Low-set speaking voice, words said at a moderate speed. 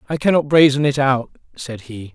Yes: low, 130 Hz; average, 195 wpm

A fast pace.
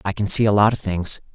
Yes: fast, 310 wpm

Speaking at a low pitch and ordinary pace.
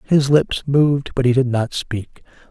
Yes: low, 130 Hz; average, 190 wpm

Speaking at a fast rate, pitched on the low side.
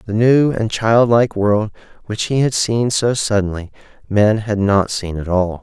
No: average, 180 wpm; low, 110 Hz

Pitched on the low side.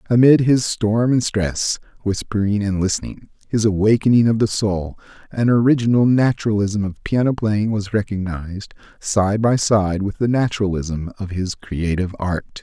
Yes: low, 105 Hz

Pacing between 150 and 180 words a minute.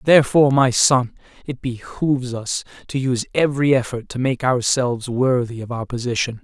Yes: average, 160 wpm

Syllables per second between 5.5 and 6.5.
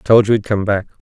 Yes: 5.6 syllables/s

